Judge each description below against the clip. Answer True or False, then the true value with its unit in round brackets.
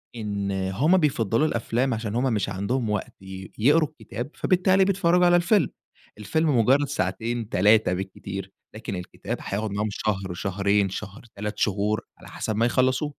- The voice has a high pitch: False (110 Hz)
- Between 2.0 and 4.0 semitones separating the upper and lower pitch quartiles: False (5.5 semitones)